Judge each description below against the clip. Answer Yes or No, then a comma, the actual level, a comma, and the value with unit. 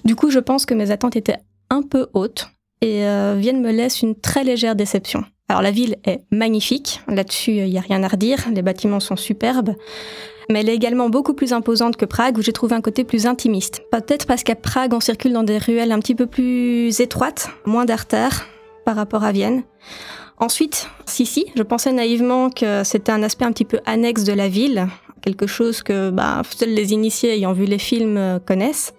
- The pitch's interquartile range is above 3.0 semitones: No, average, 2.7 semitones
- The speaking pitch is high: Yes, high, 230 Hz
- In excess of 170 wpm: Yes, average, 210 wpm